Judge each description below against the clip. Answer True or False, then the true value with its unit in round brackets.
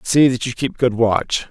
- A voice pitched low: True (120 Hz)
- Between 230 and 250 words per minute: True (240 wpm)